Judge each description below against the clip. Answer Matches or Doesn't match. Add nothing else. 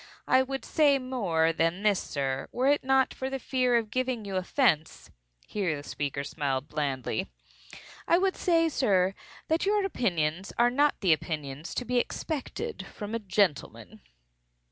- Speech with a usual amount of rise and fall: Doesn't match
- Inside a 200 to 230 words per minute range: Doesn't match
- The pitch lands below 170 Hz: Doesn't match